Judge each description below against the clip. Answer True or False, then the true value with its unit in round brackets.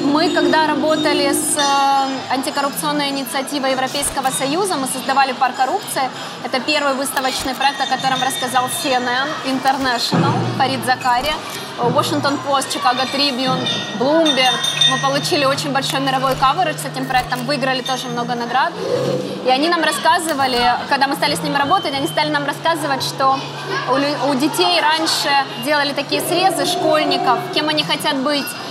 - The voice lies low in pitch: False (275 Hz)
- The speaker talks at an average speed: True (140 wpm)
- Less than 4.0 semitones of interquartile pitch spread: True (2.7 semitones)